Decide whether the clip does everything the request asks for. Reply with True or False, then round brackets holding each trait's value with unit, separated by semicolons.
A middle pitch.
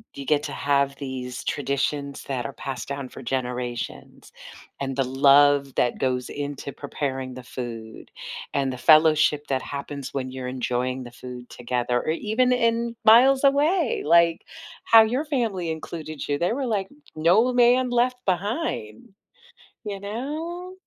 True (145 Hz)